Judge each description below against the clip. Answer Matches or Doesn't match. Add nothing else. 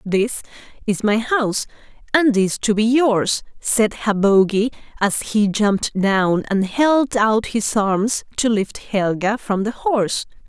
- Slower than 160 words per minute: Matches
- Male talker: Doesn't match